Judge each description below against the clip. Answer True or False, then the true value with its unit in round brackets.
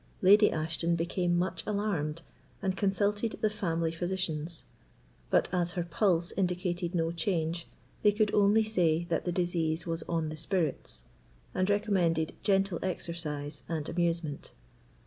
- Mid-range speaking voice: True (175 Hz)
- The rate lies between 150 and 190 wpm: False (135 wpm)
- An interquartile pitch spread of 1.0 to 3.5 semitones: True (2.9 semitones)